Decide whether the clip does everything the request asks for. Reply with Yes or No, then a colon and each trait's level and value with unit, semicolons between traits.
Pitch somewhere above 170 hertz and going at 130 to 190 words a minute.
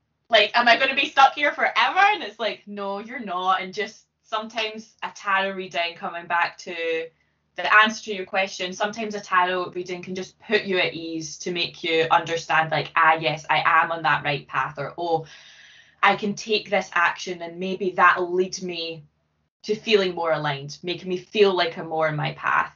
No: medium, 185 Hz; fast, 205 wpm